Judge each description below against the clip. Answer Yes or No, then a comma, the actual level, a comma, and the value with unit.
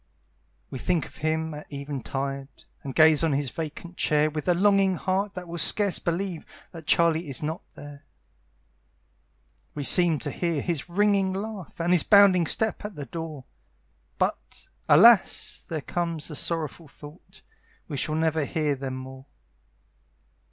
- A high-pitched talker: No, medium, 160 Hz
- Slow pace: No, average, 150 wpm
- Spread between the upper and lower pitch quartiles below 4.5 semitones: Yes, average, 3.5 semitones